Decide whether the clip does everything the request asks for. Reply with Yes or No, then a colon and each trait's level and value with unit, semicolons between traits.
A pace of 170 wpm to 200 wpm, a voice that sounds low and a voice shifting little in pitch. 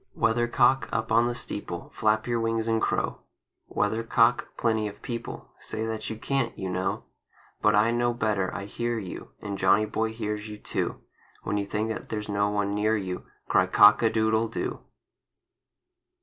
Yes: average, 175 wpm; low, 110 Hz; narrow, 1.8 semitones